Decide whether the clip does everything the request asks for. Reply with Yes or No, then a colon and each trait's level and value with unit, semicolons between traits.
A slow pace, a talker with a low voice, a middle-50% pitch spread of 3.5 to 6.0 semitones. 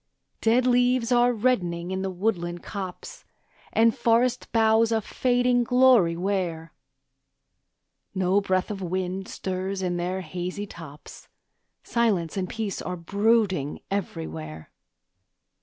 No: slow, 115 wpm; high, 195 Hz; average, 4.4 semitones